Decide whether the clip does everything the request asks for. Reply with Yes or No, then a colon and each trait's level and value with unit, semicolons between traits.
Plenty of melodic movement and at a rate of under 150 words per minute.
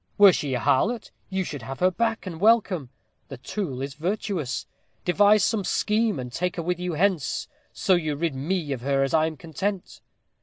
No: wide, 6.0 semitones; average, 190 wpm